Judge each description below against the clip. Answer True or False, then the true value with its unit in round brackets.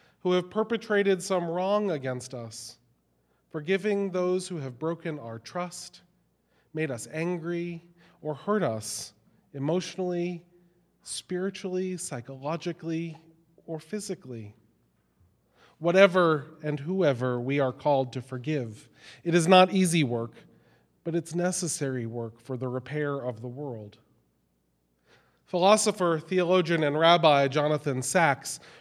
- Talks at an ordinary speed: False (110 wpm)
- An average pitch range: False (5.7 semitones)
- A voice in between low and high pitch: True (160 Hz)